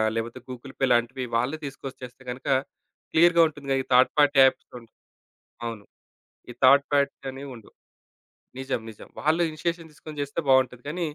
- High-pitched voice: No, low, 135 Hz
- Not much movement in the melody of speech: No, average, 3.2 semitones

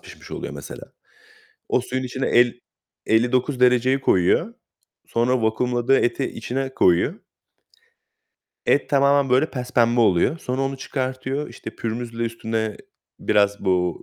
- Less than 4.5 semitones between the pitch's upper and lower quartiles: Yes, average, 2.7 semitones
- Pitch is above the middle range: No, low, 125 Hz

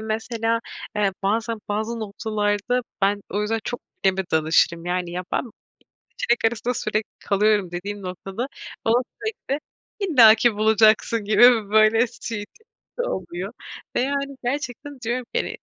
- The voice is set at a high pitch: Yes, high, 220 Hz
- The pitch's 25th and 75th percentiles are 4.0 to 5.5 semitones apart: No, average, 3.1 semitones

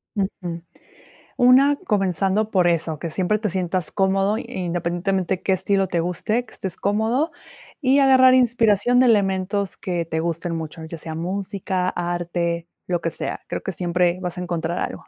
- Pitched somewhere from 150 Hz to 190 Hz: Yes, medium, 185 Hz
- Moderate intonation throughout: Yes, average, 3.5 semitones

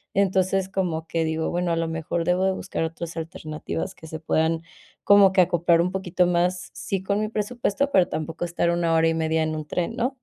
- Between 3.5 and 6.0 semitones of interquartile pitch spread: No, average, 2.8 semitones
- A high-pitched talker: No, medium, 175 Hz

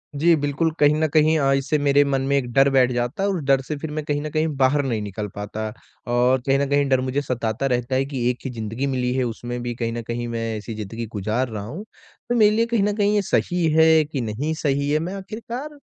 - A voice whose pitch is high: No, low, 135 Hz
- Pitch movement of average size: Yes, average, 4.2 semitones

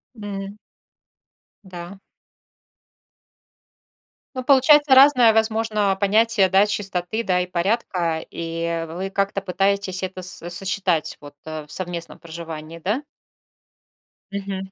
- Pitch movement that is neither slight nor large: Yes, average, 3.4 semitones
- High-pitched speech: Yes, high, 195 Hz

